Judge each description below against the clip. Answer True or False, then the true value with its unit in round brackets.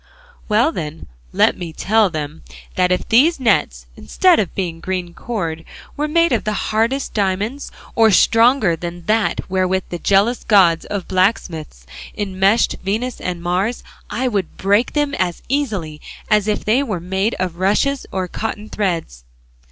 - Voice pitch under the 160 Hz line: False (195 Hz)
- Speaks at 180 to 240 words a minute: False (155 wpm)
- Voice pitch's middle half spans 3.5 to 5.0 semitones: True (4.4 semitones)